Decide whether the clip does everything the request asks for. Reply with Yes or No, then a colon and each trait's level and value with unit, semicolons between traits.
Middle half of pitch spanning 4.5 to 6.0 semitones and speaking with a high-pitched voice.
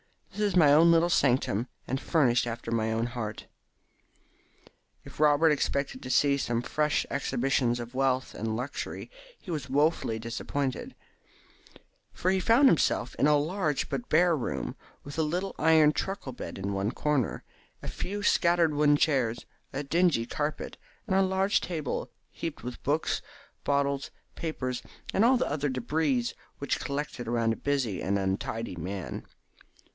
No: average, 5.0 semitones; medium, 140 Hz